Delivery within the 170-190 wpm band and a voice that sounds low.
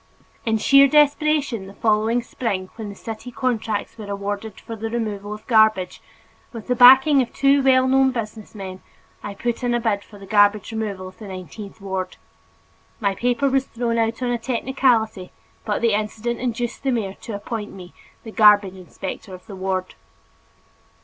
No: average, 175 wpm; high, 220 Hz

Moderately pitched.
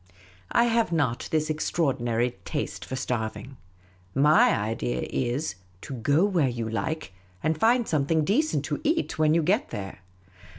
Yes: medium, 150 Hz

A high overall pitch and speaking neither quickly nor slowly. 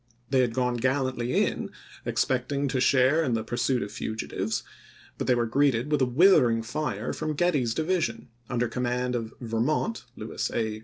No: low, 125 Hz; average, 175 wpm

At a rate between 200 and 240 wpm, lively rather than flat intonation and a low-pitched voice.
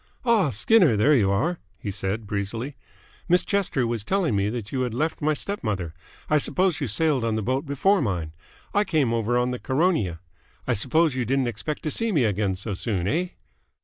Yes: fast, 205 wpm; wide, 7.0 semitones; low, 125 Hz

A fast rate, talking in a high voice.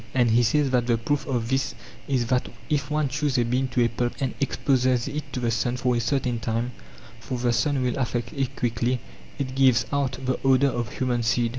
No: fast, 220 wpm; low, 125 Hz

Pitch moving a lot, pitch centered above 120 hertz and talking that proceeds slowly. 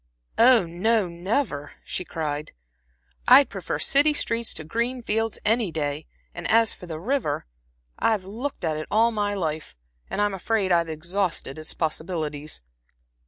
No: wide, 6.2 semitones; high, 190 Hz; average, 150 wpm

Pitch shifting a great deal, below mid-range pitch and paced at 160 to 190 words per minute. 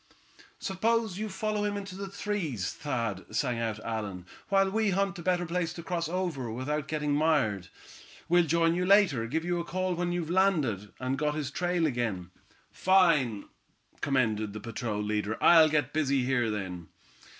No: wide, 7.9 semitones; medium, 155 Hz; average, 165 wpm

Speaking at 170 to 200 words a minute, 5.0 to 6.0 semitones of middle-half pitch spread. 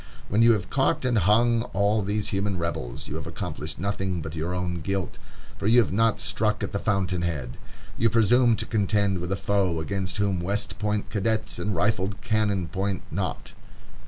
No: average, 190 wpm; average, 2.9 semitones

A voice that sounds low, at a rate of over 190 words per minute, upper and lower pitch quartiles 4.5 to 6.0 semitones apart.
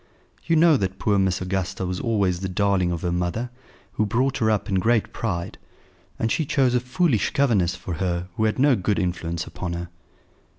Yes: low, 100 Hz; average, 200 wpm; average, 5.0 semitones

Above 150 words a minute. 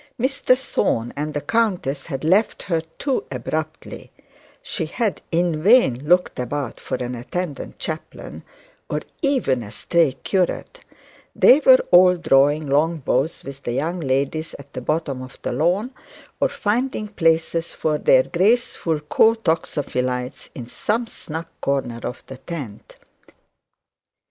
No: average, 140 wpm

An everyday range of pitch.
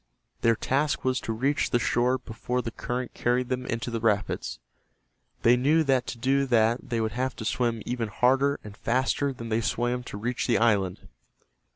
No: narrow, 2.1 semitones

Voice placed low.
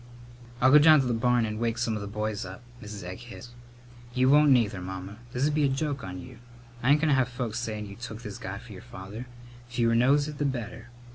Yes: low, 120 Hz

